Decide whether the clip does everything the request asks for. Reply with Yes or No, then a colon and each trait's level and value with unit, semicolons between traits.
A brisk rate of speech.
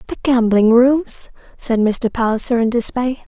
No: average, 145 wpm